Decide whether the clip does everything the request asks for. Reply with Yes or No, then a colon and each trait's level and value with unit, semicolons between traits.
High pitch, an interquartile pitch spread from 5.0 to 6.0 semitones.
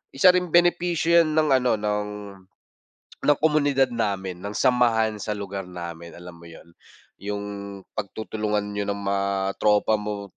No: low, 105 Hz; average, 5.3 semitones